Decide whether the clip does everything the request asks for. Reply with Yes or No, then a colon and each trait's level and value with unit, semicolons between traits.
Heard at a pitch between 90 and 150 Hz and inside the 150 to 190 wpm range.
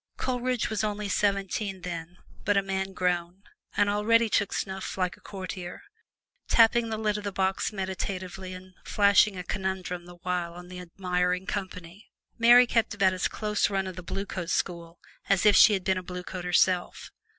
No: high, 190 Hz; average, 185 wpm